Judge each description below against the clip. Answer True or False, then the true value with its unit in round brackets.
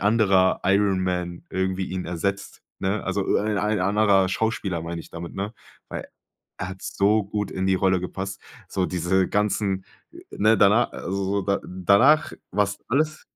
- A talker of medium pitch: False (95 Hz)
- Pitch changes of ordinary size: False (1.9 semitones)